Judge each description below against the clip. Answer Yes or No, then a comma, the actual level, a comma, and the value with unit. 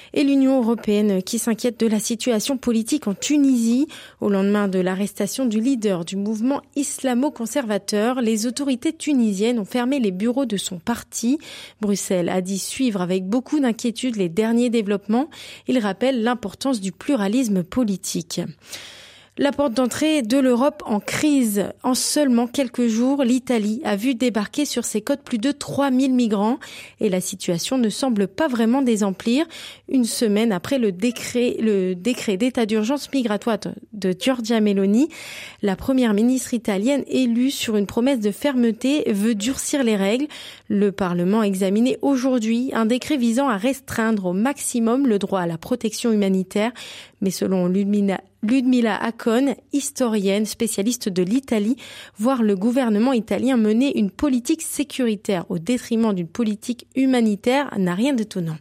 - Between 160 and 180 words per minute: No, average, 150 wpm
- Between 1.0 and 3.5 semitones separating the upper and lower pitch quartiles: No, average, 4.1 semitones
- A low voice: No, high, 235 Hz